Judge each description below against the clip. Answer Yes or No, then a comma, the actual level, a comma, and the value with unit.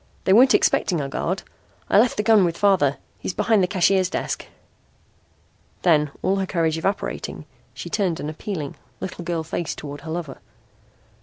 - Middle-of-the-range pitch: Yes, medium, 180 Hz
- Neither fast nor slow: Yes, average, 165 wpm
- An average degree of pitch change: Yes, average, 3.7 semitones